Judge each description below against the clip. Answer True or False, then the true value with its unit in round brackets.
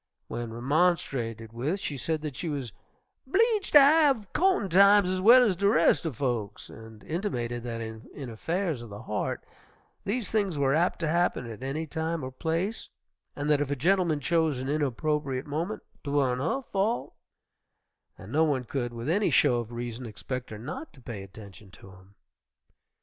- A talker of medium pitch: True (145 Hz)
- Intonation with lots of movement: True (7.1 semitones)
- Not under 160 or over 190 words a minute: True (175 wpm)